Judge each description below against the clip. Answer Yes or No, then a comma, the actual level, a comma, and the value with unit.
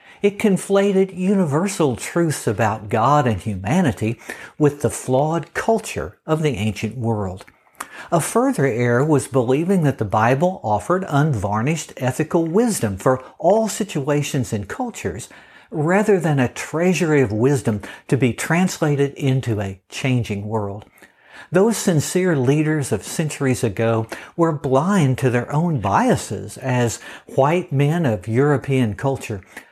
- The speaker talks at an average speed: No, slow, 130 wpm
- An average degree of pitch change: No, wide, 6.6 semitones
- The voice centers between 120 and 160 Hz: Yes, medium, 140 Hz